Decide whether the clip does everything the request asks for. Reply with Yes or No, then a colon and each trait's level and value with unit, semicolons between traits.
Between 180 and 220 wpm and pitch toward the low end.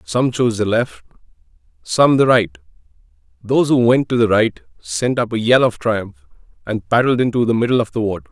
Yes: average, 195 wpm; low, 120 Hz